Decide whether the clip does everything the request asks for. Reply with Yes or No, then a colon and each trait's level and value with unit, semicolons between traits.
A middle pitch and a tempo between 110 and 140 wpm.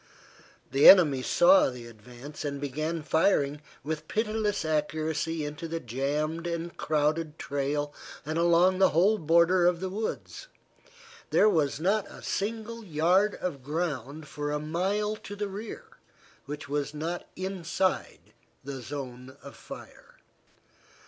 Yes: medium, 160 Hz; slow, 135 wpm